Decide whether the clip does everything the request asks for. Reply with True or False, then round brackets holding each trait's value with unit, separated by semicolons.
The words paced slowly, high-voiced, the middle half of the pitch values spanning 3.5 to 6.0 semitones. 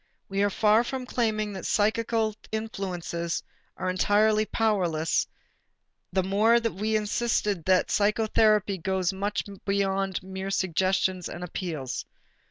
False (120 wpm; 200 Hz; 2.6 semitones)